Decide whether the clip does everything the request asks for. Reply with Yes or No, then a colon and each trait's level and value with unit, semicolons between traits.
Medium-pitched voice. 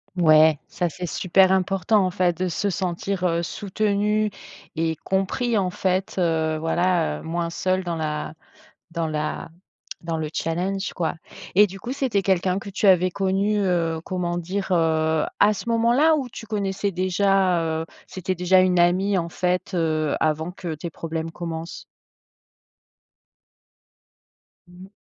Yes: medium, 180 Hz